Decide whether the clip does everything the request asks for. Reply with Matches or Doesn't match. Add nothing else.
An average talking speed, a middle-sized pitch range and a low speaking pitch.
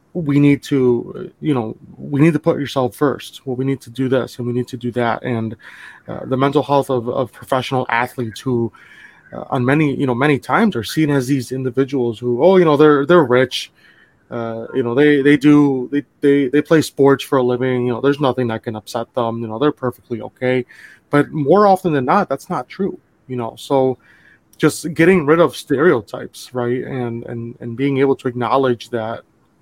Doesn't match